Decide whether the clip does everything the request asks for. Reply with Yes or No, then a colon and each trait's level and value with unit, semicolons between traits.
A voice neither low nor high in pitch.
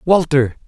Yes: medium, 145 Hz